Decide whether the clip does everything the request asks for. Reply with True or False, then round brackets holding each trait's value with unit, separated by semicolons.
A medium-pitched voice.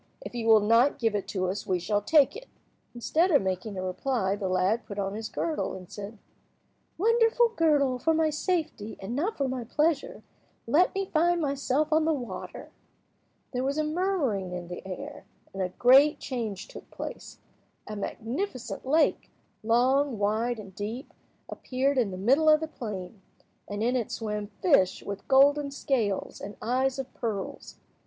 False (245 Hz)